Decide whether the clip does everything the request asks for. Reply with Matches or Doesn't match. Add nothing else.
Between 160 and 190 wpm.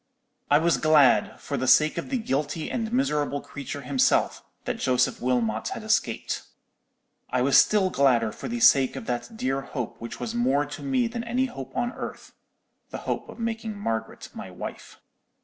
Matches